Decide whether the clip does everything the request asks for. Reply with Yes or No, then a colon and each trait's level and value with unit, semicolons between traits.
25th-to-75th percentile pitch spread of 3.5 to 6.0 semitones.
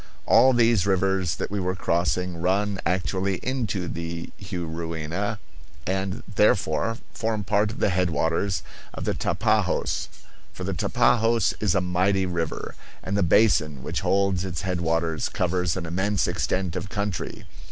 No: average, 3.0 semitones